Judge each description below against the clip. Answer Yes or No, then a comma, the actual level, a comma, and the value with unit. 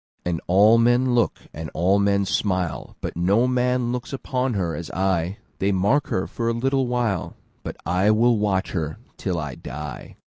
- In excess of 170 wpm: No, average, 160 wpm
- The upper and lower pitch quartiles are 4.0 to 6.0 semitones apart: Yes, average, 5.2 semitones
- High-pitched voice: No, low, 100 Hz